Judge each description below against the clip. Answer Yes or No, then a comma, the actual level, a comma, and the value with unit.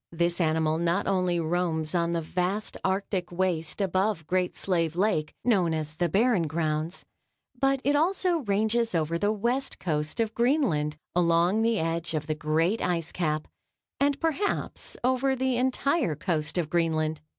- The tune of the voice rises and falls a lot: Yes, wide, 5.7 semitones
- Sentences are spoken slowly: No, average, 155 wpm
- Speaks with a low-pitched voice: No, medium, 175 Hz